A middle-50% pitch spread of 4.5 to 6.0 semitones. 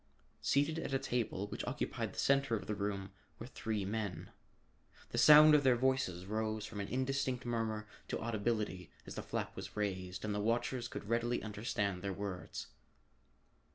No: average, 3.6 semitones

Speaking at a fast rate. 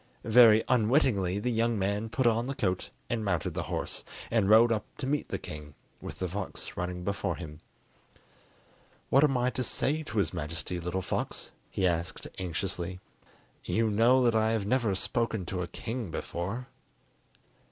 No: average, 170 wpm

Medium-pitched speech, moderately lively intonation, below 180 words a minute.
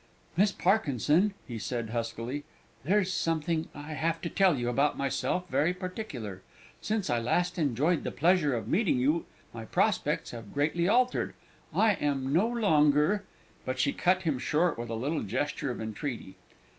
No: medium, 150 Hz; wide, 6.4 semitones; average, 170 wpm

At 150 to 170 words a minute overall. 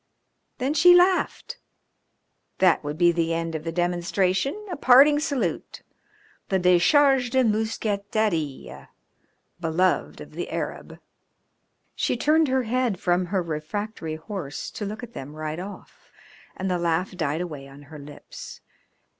No: average, 140 wpm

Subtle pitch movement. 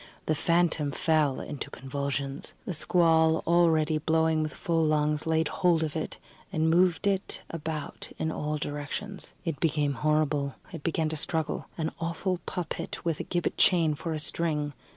Yes: narrow, 1.9 semitones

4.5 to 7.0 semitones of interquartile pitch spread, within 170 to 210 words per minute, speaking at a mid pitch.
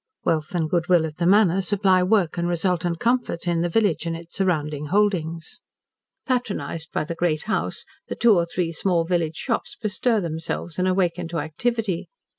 No: average, 3.0 semitones; average, 180 wpm; medium, 175 Hz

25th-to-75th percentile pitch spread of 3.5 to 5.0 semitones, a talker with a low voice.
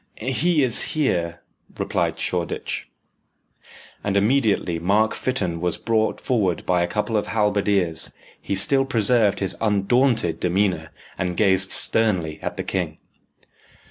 Yes: average, 4.2 semitones; low, 100 Hz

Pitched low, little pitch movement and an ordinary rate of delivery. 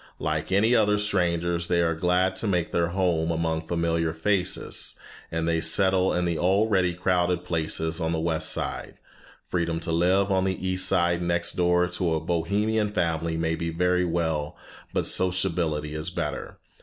Yes: very low, 85 Hz; narrow, 2.0 semitones; average, 170 wpm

